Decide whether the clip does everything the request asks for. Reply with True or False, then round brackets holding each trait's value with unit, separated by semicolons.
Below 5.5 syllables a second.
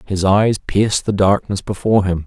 True (5.2 syllables/s)